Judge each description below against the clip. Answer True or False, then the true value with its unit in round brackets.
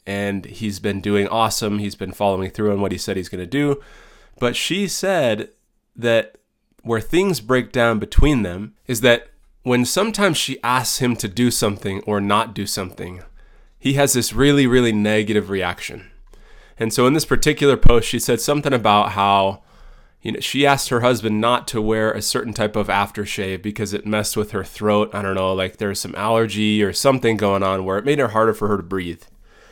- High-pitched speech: False (110 Hz)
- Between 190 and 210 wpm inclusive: True (200 wpm)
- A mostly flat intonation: False (3.6 semitones)